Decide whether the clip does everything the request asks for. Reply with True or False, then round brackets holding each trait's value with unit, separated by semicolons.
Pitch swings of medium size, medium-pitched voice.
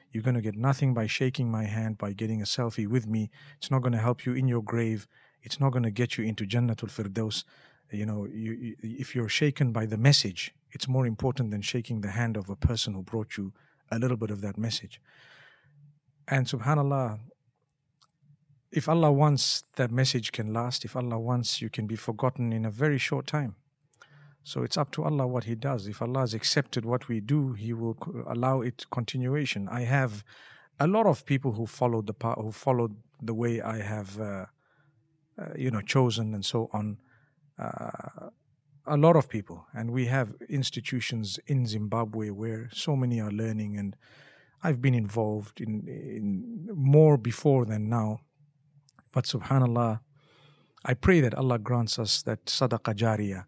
False (3.9 semitones; 120 Hz)